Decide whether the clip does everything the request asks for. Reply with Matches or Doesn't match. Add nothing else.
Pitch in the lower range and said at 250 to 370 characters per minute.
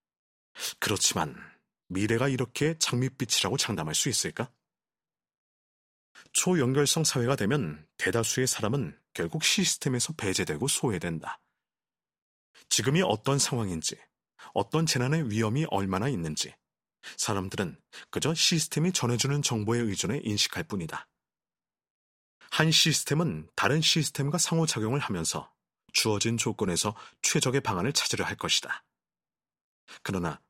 Matches